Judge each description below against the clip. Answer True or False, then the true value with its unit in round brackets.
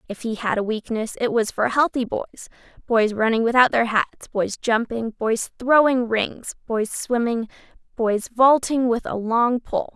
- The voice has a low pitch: False (230 Hz)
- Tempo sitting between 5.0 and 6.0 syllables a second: False (4.3 syllables/s)